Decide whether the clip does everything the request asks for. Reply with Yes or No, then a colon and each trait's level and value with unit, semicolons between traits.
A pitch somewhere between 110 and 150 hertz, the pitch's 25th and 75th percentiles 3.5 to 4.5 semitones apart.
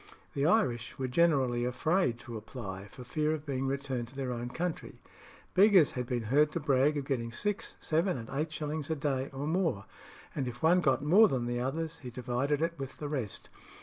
Yes: medium, 140 Hz; average, 4.2 semitones